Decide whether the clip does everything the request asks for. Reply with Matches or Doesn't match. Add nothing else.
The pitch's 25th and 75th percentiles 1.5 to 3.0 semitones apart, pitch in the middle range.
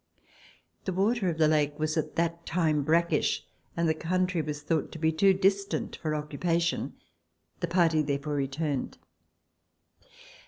Matches